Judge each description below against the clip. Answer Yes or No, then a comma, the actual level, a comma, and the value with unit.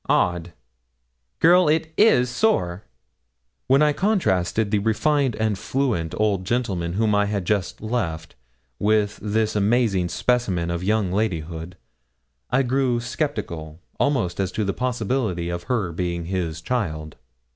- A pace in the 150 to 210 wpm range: No, slow, 135 wpm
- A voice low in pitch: Yes, low, 105 Hz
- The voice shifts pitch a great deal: Yes, wide, 5.9 semitones